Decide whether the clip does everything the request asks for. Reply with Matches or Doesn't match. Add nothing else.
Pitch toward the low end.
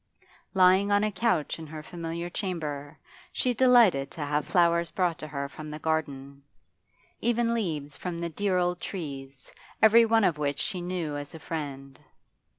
Doesn't match